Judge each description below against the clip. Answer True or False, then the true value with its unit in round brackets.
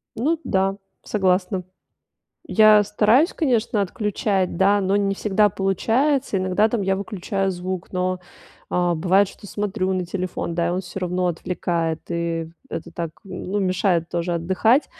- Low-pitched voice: False (190 Hz)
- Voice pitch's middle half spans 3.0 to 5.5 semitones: False (2.5 semitones)